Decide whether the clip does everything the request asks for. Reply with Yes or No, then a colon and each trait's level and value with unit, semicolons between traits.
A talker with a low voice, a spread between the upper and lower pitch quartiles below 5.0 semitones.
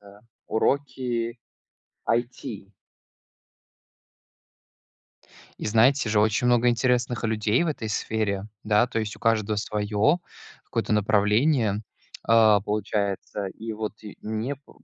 Yes: low, 110 Hz; narrow, 2.5 semitones